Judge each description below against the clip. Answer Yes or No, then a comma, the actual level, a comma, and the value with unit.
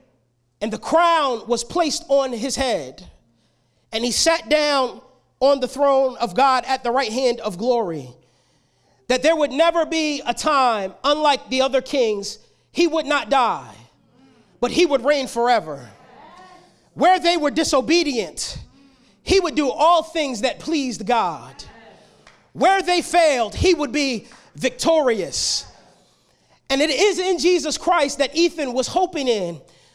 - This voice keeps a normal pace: Yes, average, 145 wpm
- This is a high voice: Yes, very high, 275 Hz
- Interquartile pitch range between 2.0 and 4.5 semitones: No, average, 5.2 semitones